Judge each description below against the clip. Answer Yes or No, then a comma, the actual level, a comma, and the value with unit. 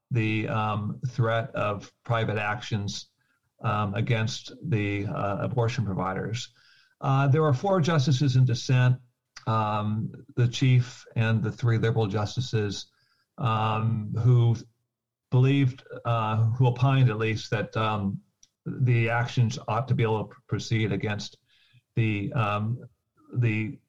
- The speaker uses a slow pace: Yes, slow, 125 wpm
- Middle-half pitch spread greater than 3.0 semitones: No, narrow, 2.6 semitones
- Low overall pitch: Yes, low, 115 Hz